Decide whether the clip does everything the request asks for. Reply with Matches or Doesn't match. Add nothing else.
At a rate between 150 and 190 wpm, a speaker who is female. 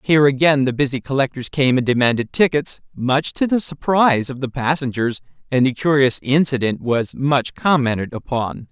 Doesn't match